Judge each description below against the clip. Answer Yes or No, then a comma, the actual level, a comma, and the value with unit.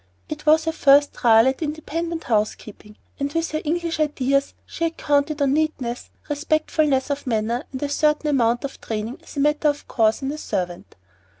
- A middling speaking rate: Yes, average, 185 wpm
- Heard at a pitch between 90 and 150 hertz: No, very high, 285 Hz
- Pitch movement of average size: Yes, average, 3.8 semitones